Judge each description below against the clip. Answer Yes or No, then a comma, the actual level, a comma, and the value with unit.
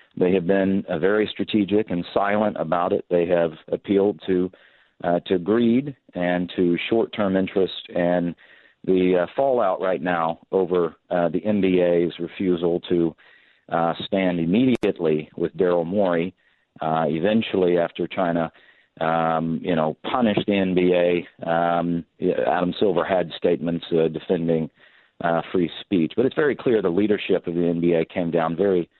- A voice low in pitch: Yes, very low, 90 Hz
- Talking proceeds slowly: No, average, 145 wpm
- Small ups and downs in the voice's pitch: Yes, narrow, 2.2 semitones